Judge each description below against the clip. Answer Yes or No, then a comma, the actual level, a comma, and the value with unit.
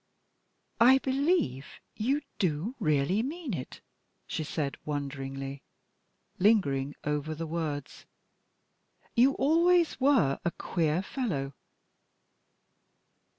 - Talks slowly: Yes, slow, 90 wpm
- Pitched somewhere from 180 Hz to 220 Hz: No, medium, 165 Hz